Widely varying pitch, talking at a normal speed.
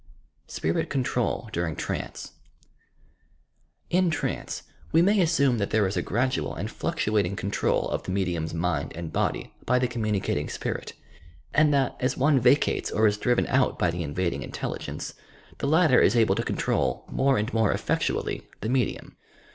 Yes: wide, 6.4 semitones; average, 160 wpm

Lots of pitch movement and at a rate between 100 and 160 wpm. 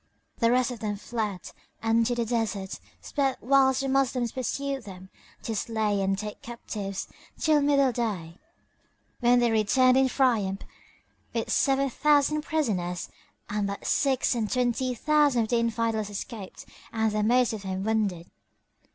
No: average, 4.0 semitones; average, 145 wpm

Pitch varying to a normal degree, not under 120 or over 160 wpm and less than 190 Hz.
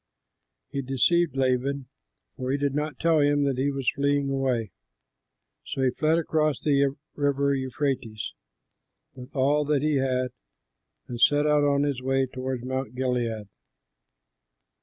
No: narrow, 2.0 semitones; average, 140 wpm; low, 135 Hz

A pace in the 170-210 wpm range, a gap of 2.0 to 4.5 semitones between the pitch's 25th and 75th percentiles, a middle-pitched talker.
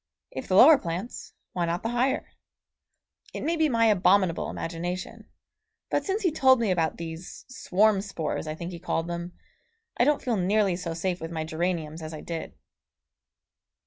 No: average, 175 wpm; wide, 5.4 semitones; medium, 180 Hz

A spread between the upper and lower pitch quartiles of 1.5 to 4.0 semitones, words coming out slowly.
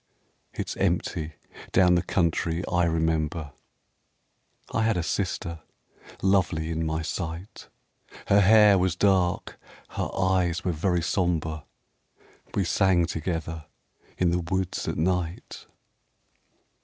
Yes: narrow, 2.5 semitones; slow, 115 wpm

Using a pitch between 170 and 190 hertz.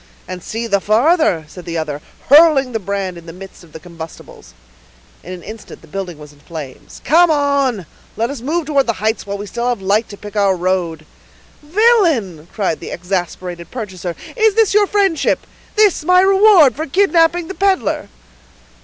No: high, 215 Hz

